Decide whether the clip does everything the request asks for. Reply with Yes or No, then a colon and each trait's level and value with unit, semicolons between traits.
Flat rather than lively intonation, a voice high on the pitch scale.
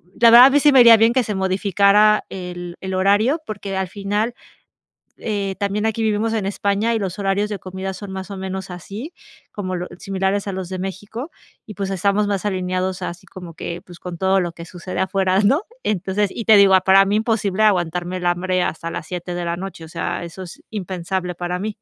Yes: narrow, 2.3 semitones; high, 195 Hz